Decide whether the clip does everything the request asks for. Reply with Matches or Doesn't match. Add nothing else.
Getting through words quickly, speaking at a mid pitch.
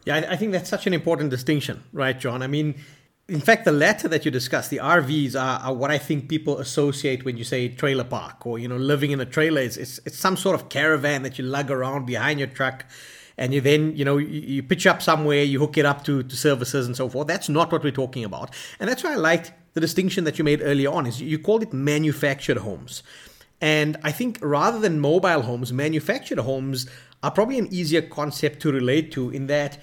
Matches